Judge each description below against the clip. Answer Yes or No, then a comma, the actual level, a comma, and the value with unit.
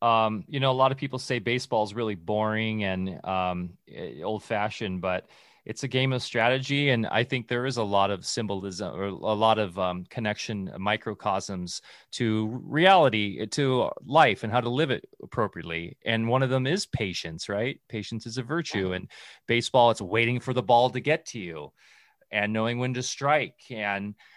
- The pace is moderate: Yes, average, 185 wpm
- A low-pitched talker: Yes, low, 110 Hz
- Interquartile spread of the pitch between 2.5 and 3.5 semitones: No, average, 3.9 semitones